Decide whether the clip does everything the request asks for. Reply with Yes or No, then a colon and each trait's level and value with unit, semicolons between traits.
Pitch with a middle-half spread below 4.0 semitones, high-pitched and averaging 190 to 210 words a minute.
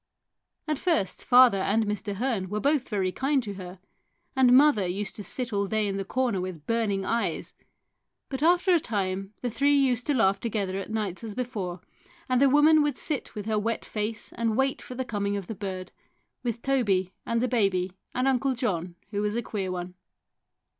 No: average, 4.7 semitones; high, 220 Hz; average, 200 wpm